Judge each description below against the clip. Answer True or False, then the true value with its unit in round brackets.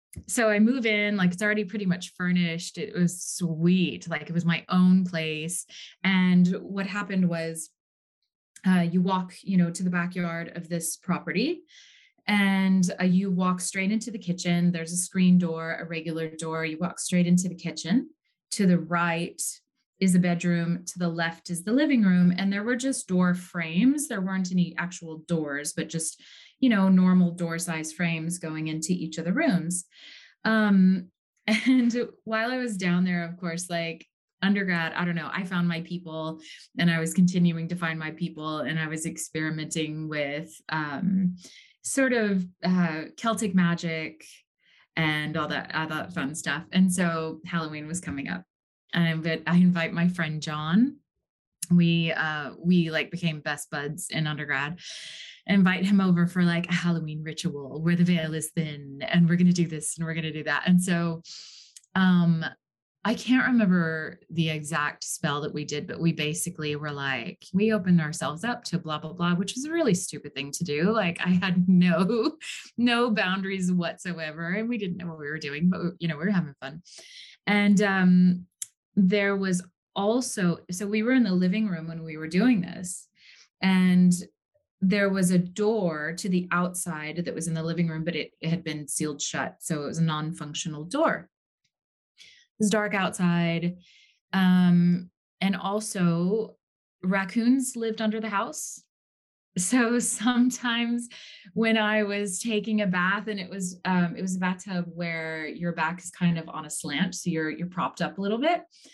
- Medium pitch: True (180 Hz)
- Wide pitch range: False (3.3 semitones)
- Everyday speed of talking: True (180 wpm)